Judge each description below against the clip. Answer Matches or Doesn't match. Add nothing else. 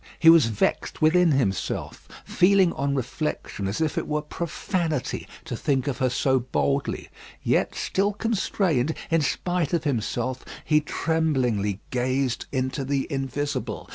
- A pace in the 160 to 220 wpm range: Doesn't match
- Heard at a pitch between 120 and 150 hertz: Matches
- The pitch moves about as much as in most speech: Matches